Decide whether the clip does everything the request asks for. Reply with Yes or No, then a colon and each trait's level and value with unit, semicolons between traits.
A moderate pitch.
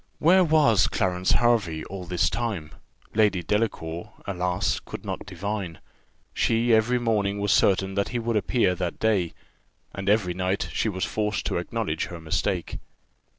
No: low, 100 Hz